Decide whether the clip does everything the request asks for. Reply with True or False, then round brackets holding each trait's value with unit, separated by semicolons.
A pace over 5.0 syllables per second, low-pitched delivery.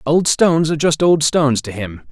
False (5.6 syllables/s; 145 Hz)